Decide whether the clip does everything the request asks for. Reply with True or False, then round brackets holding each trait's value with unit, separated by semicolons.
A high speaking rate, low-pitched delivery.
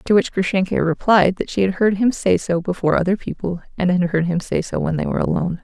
False (255 wpm; 185 Hz)